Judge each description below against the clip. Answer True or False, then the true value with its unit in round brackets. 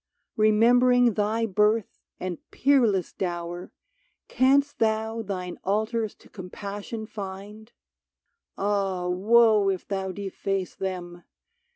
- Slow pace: True (95 wpm)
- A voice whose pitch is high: True (205 Hz)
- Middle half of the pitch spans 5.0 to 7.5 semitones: False (2.9 semitones)